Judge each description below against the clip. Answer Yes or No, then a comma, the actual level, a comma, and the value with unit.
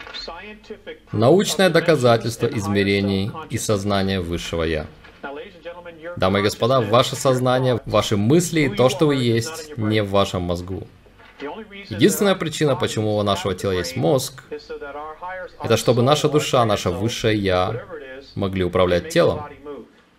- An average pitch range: No, wide, 7.4 semitones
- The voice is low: Yes, low, 115 Hz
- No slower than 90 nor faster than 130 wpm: Yes, average, 120 wpm